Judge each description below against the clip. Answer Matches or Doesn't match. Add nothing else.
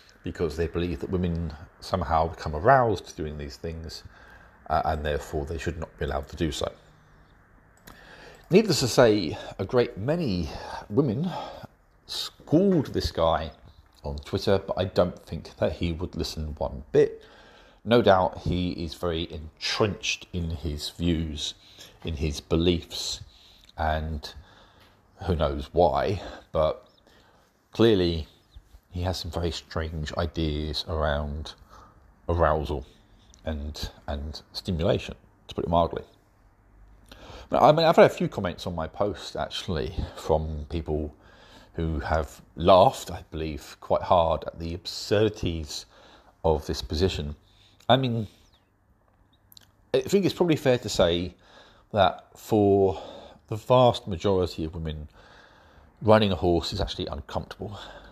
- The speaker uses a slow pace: Matches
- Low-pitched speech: Matches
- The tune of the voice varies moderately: Matches